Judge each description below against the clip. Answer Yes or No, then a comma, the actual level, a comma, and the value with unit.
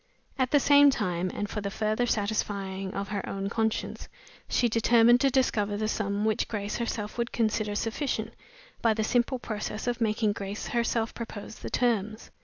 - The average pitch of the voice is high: Yes, high, 220 Hz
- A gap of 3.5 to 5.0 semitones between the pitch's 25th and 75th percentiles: No, narrow, 2.4 semitones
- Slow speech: No, average, 175 wpm